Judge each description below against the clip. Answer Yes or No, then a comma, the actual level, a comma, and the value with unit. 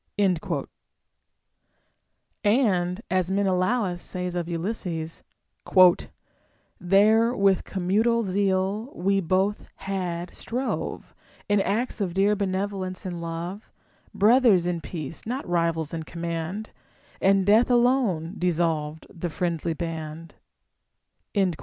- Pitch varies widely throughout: No, average, 3.3 semitones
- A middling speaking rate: No, slow, 110 wpm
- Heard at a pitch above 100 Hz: Yes, medium, 185 Hz